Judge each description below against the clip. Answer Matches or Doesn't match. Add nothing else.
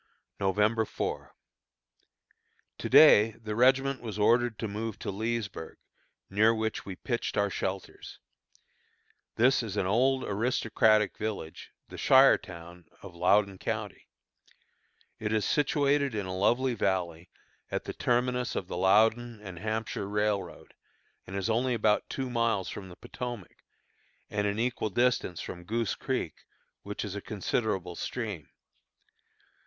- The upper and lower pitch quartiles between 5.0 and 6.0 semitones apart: Doesn't match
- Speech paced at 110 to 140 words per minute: Matches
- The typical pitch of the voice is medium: Doesn't match